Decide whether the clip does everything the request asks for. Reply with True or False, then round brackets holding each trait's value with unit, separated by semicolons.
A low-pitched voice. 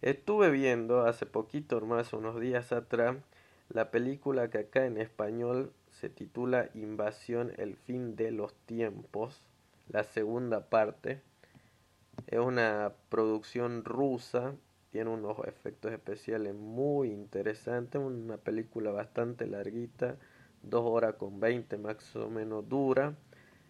True (115 Hz)